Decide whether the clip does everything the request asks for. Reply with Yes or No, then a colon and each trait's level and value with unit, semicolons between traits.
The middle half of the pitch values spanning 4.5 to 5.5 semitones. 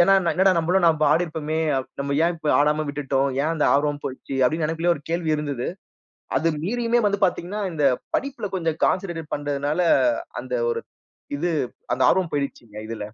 No: average, 3.4 semitones